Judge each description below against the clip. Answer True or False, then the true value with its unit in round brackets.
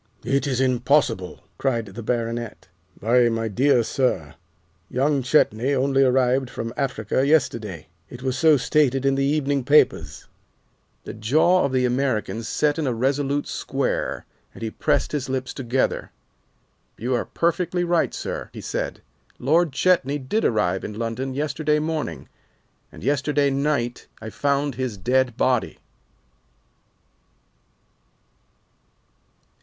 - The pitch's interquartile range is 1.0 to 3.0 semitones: False (3.4 semitones)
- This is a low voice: True (130 Hz)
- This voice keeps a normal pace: False (130 wpm)